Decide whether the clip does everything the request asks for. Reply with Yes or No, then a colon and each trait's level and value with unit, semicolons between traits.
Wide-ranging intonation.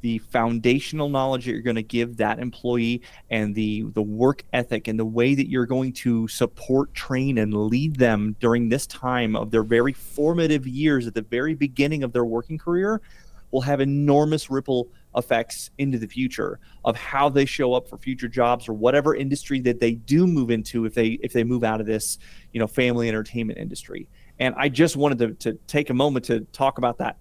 No: average, 3.0 semitones